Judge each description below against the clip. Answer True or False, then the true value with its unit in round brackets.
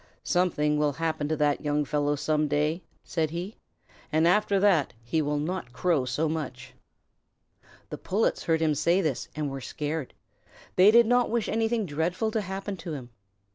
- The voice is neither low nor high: True (160 Hz)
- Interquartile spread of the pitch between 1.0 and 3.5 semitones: False (4.1 semitones)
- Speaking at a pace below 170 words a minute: False (175 wpm)